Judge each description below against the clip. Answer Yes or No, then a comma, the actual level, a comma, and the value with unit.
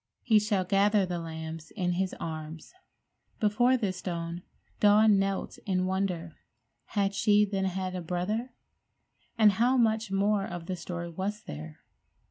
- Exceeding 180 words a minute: No, average, 145 wpm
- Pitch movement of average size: Yes, average, 3.2 semitones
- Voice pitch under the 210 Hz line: Yes, high, 190 Hz